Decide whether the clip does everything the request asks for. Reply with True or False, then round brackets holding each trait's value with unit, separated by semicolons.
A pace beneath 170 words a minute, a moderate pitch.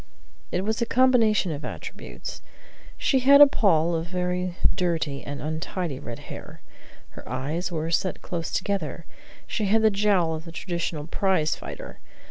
True (155 wpm; 175 Hz)